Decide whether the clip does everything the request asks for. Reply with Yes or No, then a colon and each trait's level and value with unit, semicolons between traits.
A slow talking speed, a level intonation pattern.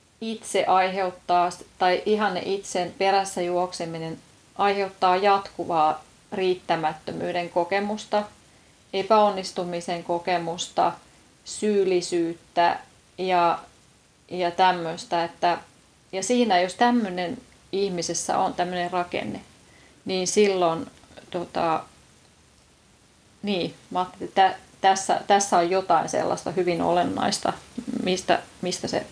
Yes: slow, 90 wpm; narrow, 2.1 semitones